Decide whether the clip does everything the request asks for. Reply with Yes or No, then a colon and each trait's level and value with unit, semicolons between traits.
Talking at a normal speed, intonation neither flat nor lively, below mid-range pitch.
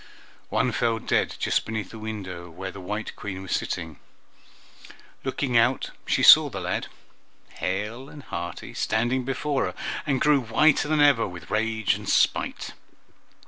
No: average, 150 wpm; wide, 5.7 semitones; low, 110 Hz